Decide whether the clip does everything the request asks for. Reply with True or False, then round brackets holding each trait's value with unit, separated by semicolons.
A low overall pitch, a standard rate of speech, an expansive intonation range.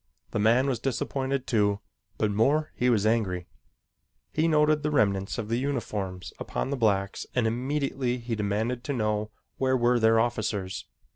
False (115 Hz; 160 wpm; 4.0 semitones)